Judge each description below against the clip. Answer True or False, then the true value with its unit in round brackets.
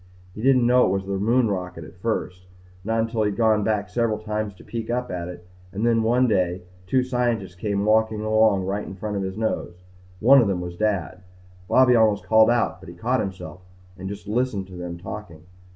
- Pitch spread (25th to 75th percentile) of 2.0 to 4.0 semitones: True (3.4 semitones)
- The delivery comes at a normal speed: False (215 wpm)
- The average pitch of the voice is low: True (105 Hz)